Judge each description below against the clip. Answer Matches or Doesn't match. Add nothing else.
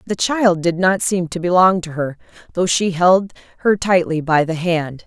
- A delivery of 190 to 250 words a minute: Matches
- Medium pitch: Matches